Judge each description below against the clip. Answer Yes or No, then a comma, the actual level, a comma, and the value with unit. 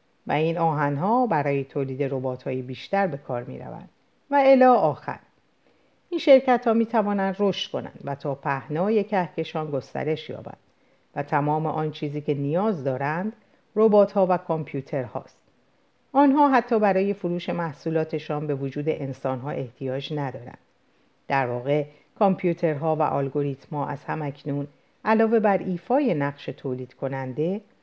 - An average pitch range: No, wide, 6.0 semitones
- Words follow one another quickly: No, average, 145 wpm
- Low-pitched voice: No, medium, 155 Hz